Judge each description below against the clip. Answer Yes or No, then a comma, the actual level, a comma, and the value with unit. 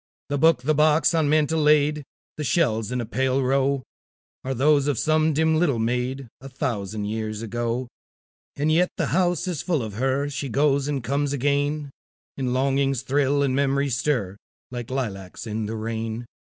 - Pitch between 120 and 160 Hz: Yes, low, 135 Hz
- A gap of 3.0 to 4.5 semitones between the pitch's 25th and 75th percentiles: Yes, average, 3.7 semitones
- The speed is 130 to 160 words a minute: No, average, 175 wpm